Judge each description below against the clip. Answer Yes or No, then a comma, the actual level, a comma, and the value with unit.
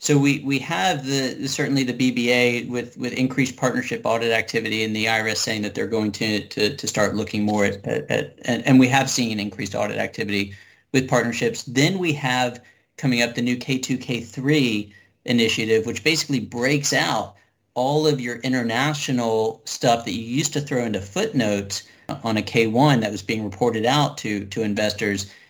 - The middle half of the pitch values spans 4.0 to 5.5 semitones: No, average, 3.5 semitones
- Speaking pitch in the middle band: No, low, 120 Hz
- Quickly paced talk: No, average, 180 wpm